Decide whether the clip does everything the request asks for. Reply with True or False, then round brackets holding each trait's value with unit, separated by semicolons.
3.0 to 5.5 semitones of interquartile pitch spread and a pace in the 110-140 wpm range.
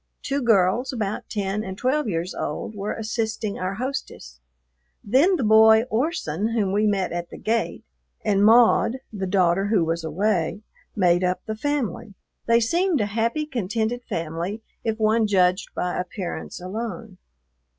False (3.8 semitones; 150 wpm)